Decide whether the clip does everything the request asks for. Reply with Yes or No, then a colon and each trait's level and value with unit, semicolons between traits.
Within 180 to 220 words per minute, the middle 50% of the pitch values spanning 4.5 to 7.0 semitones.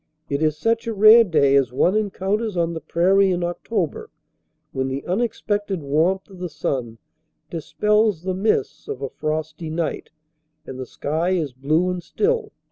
No: average, 165 wpm; average, 5.2 semitones